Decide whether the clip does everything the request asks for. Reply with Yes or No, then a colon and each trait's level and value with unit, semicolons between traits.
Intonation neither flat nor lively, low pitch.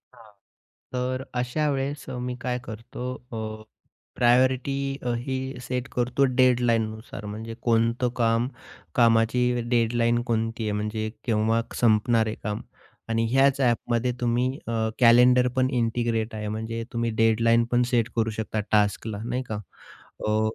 No: narrow, 1.8 semitones; low, 115 Hz